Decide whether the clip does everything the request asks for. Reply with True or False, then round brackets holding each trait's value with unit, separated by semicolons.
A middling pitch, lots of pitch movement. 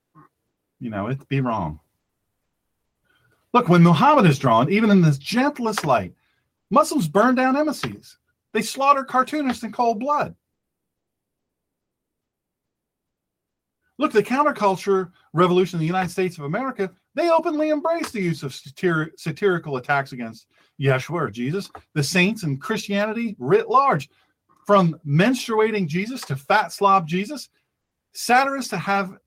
False (195 Hz; 8.1 semitones)